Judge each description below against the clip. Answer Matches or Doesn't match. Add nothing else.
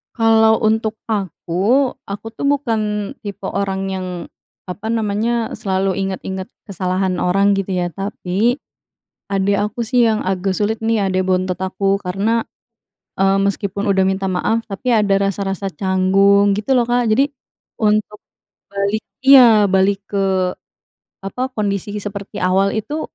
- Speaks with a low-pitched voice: Doesn't match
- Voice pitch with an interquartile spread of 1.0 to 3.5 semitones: Matches